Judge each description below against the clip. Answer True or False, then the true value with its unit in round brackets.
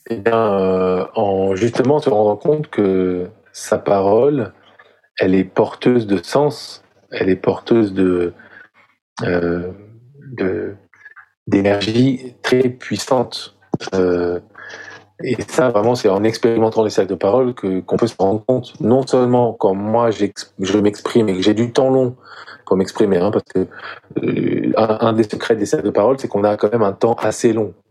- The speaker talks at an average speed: True (165 wpm)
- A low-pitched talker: True (110 Hz)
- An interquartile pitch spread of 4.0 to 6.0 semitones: True (4.4 semitones)